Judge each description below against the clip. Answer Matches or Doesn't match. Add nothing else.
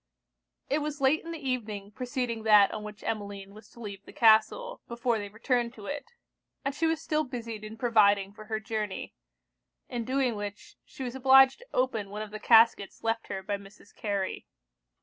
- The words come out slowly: Doesn't match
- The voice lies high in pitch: Matches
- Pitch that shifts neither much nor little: Matches